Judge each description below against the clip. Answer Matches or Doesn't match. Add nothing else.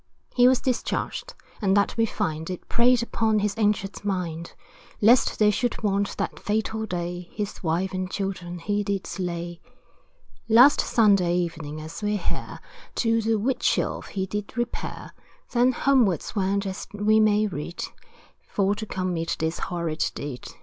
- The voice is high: Matches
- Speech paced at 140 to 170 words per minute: Matches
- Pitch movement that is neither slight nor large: Matches